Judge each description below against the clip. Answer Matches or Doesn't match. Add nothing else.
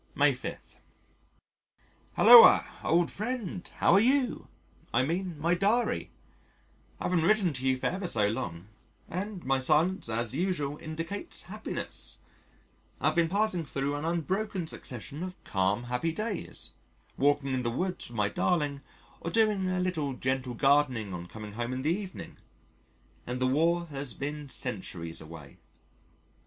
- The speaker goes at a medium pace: Matches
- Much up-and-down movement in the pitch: Matches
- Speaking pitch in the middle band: Matches